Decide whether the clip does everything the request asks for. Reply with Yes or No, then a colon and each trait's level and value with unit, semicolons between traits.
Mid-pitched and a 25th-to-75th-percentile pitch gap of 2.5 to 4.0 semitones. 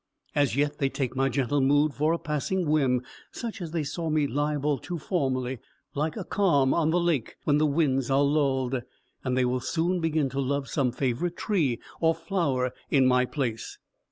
Yes: medium, 145 Hz; average, 3.4 semitones